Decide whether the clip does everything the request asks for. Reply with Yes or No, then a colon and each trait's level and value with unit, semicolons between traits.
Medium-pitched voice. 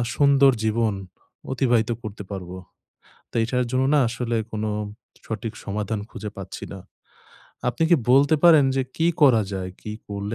No: low, 115 Hz